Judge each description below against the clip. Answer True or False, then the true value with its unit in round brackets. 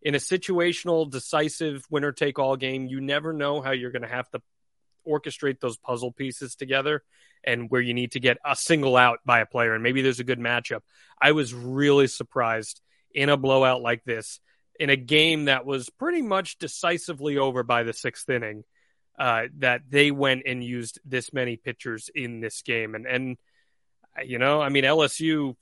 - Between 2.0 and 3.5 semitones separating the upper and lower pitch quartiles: True (2.9 semitones)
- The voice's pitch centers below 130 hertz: False (135 Hz)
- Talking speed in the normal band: True (190 wpm)